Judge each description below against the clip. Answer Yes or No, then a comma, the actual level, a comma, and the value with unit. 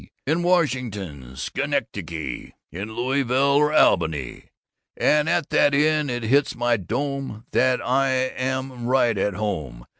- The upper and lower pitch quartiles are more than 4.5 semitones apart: Yes, wide, 5.5 semitones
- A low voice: Yes, low, 130 Hz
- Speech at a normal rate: No, slow, 130 wpm